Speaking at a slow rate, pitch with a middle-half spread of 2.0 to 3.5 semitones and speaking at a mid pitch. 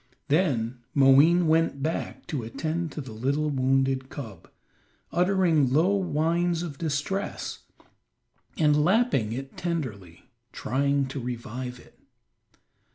No: slow, 110 wpm; average, 4.4 semitones; medium, 145 Hz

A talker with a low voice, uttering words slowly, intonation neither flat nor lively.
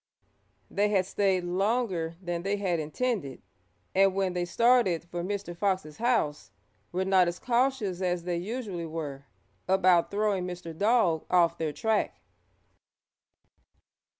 No: medium, 185 Hz; slow, 130 wpm; average, 3.1 semitones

